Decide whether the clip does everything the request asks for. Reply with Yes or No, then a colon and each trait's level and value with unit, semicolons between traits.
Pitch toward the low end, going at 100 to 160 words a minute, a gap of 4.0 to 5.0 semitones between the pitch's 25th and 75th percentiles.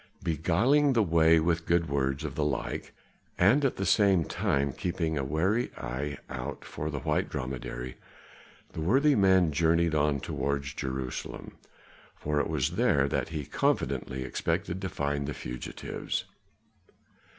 Yes: very low, 80 Hz; average, 145 wpm; average, 4.3 semitones